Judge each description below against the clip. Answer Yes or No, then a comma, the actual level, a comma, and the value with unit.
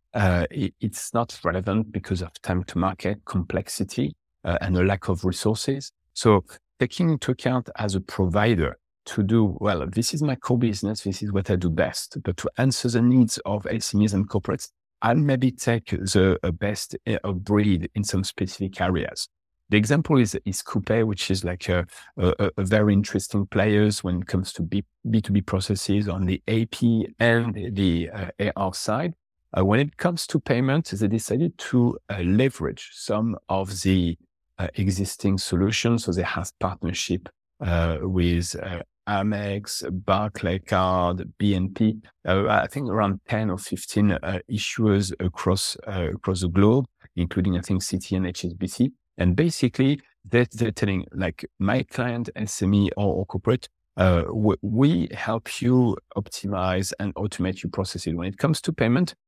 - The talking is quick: No, average, 165 wpm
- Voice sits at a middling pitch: No, low, 100 Hz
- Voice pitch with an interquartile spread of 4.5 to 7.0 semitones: No, average, 3.3 semitones